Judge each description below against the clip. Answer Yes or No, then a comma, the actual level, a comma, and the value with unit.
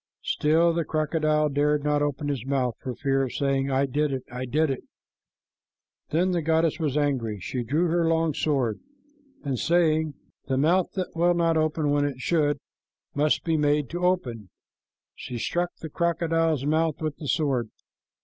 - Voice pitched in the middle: Yes, medium, 150 Hz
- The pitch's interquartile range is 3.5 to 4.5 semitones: No, average, 3.1 semitones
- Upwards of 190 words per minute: No, average, 170 wpm